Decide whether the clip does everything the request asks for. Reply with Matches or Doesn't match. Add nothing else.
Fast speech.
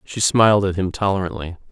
Doesn't match